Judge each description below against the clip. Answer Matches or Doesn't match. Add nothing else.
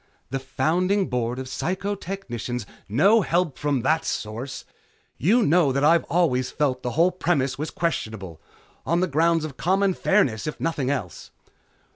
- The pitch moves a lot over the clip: Matches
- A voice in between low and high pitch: Matches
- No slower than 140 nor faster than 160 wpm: Matches